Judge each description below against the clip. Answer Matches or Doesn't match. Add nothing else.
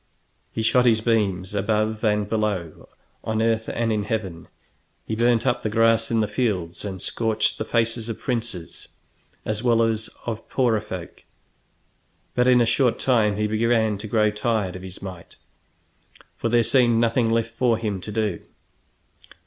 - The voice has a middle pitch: Doesn't match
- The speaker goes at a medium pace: Matches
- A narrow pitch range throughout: Matches